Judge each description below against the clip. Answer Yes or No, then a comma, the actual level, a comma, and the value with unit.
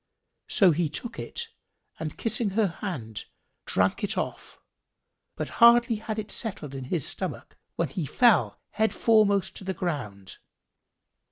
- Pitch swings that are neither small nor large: No, wide, 6.6 semitones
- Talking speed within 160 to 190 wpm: No, average, 145 wpm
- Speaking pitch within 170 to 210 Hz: Yes, high, 190 Hz